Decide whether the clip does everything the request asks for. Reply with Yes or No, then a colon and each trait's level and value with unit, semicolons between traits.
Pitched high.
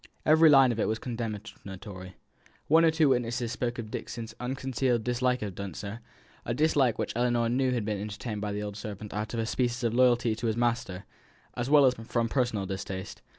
No: low, 120 Hz